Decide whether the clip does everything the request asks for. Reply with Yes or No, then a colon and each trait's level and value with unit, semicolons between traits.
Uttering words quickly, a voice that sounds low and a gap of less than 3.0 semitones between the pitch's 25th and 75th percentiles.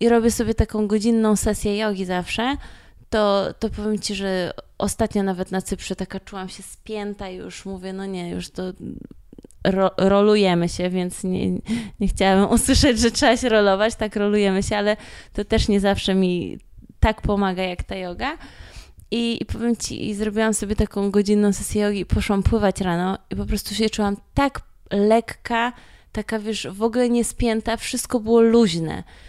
No: fast, 175 wpm; high, 205 Hz; narrow, 2.6 semitones